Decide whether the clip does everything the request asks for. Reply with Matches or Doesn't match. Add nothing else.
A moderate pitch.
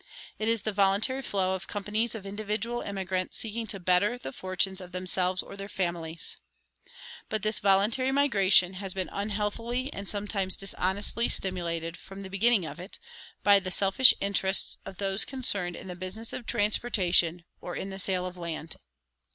Doesn't match